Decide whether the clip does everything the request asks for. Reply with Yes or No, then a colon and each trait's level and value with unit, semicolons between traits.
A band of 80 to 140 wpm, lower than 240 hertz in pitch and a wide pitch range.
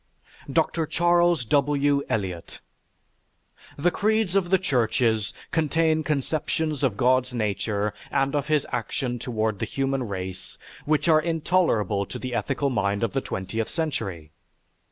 Yes: slow, 135 wpm; low, 135 Hz; wide, 6.3 semitones